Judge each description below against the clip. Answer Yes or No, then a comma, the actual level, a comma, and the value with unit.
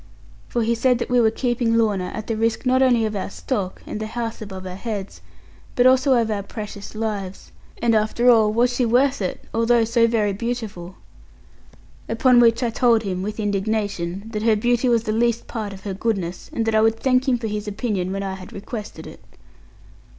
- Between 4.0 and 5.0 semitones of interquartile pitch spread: No, average, 2.8 semitones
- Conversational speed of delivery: No, fast, 210 wpm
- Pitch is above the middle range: Yes, high, 225 Hz